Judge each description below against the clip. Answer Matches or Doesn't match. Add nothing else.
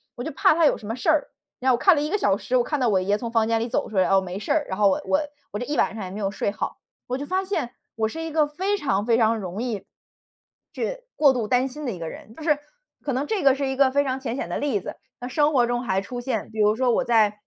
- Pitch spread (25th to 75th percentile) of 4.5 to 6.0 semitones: Matches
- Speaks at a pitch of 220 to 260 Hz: Matches